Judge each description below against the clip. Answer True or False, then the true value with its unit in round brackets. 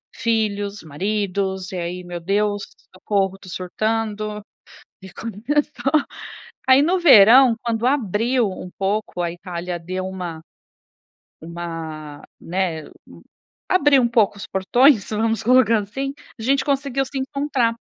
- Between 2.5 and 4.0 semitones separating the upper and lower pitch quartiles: False (5.0 semitones)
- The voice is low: False (210 Hz)